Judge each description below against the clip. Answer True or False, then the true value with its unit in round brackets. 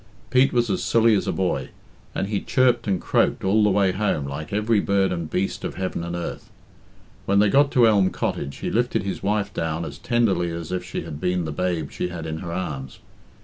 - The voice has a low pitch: True (95 Hz)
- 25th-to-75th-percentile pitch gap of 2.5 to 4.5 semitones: True (3.9 semitones)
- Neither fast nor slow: False (225 wpm)